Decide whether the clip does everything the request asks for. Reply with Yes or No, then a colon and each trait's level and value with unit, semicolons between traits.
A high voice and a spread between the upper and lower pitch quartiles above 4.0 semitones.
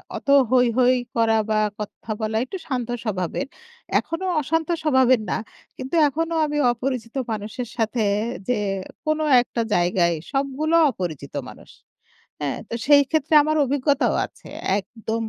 Yes: very high, 250 Hz; average, 4.7 semitones